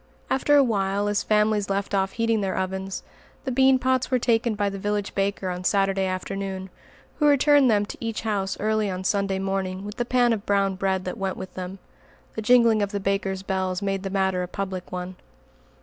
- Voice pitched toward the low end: No, high, 195 Hz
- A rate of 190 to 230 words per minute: Yes, fast, 205 wpm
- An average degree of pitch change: No, narrow, 2.3 semitones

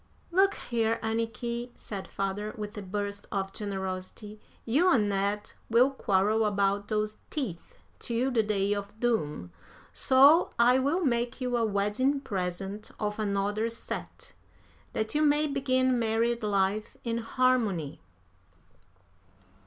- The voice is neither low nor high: No, high, 220 Hz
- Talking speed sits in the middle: No, slow, 130 wpm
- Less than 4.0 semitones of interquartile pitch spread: Yes, average, 3.4 semitones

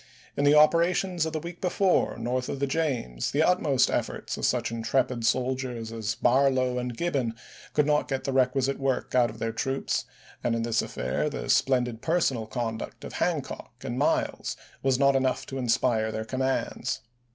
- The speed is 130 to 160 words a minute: No, average, 175 wpm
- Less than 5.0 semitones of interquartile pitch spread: Yes, average, 3.2 semitones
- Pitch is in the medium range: No, low, 130 Hz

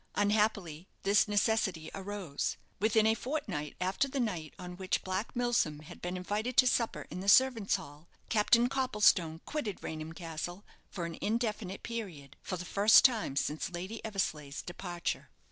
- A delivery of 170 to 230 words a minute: No, average, 155 wpm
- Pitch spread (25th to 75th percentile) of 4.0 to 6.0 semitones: Yes, average, 4.4 semitones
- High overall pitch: Yes, high, 195 Hz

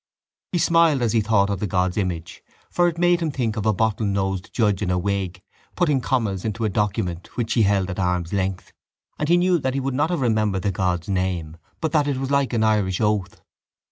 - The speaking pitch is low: Yes, low, 105 Hz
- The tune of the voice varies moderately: No, wide, 6.0 semitones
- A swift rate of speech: Yes, fast, 230 wpm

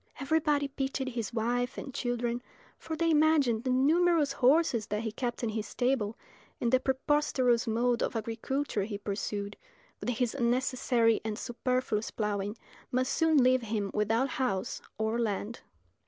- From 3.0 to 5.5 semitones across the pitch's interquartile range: Yes, average, 3.4 semitones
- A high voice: Yes, high, 245 Hz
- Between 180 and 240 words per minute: No, average, 150 wpm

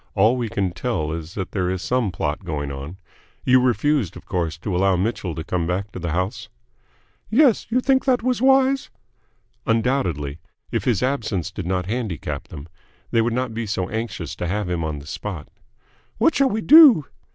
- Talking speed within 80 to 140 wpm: No, average, 190 wpm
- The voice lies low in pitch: Yes, low, 100 Hz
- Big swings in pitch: Yes, wide, 6.7 semitones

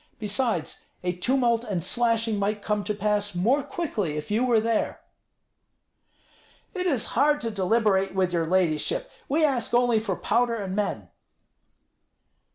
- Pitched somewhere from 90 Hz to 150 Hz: No, high, 215 Hz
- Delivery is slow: No, average, 145 wpm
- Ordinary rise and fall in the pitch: Yes, average, 3.8 semitones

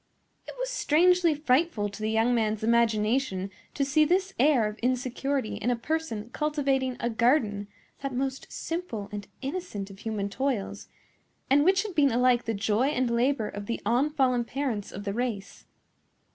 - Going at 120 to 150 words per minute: No, average, 165 wpm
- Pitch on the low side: No, very high, 250 Hz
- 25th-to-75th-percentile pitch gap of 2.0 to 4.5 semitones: No, average, 5.0 semitones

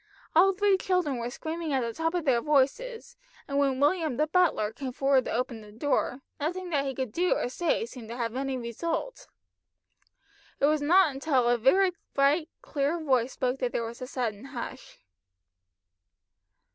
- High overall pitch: Yes, very high, 275 Hz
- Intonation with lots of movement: No, average, 4.7 semitones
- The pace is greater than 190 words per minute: No, average, 180 wpm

